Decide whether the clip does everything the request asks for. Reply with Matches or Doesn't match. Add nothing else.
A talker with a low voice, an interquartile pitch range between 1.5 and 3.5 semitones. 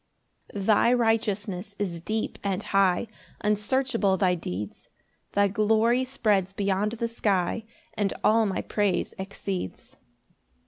Doesn't match